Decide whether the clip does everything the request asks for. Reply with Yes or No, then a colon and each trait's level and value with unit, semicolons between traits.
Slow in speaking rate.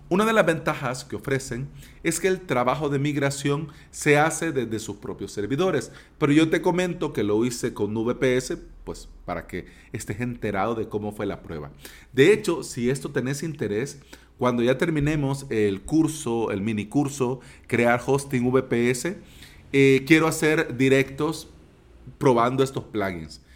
No: average, 155 wpm